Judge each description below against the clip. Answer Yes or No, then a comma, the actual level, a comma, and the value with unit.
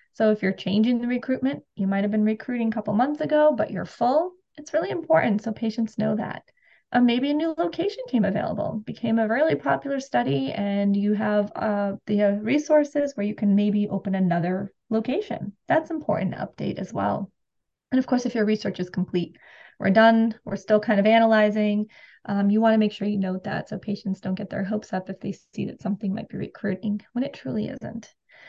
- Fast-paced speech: Yes, fast, 210 wpm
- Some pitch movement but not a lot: Yes, average, 3.5 semitones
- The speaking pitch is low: No, high, 215 Hz